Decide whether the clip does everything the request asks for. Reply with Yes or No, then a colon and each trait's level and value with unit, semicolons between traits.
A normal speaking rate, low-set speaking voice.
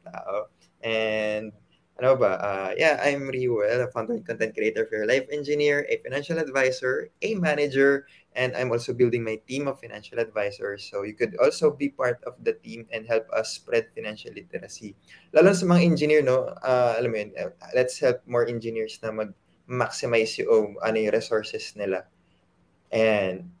No: fast, 170 wpm; low, 125 Hz